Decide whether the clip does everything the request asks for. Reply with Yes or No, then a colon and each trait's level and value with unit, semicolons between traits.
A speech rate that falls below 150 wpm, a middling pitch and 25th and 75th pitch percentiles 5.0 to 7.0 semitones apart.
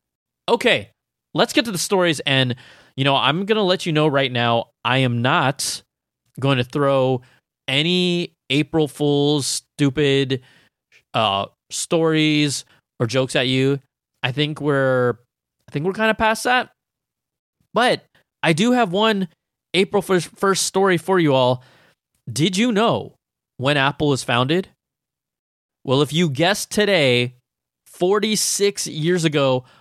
Yes: slow, 135 wpm; medium, 150 Hz; wide, 5.6 semitones